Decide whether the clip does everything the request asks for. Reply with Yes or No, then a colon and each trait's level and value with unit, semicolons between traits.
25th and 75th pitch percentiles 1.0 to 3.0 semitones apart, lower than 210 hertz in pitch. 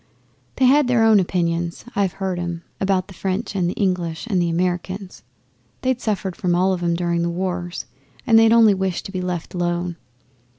Yes: narrow, 2.4 semitones; medium, 185 Hz